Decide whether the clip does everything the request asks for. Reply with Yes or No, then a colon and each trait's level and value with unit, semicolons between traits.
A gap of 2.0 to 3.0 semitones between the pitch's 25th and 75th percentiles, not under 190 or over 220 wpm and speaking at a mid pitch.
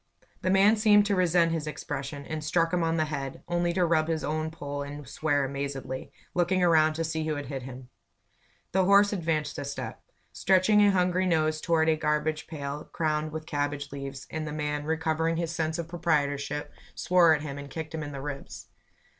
Yes: average, 2.7 semitones; average, 200 wpm; medium, 155 Hz